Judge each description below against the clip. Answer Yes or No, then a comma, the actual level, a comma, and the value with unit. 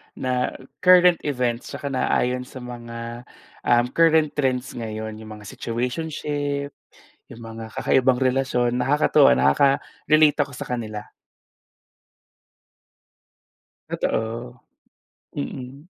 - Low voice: Yes, low, 125 Hz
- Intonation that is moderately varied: Yes, average, 3.3 semitones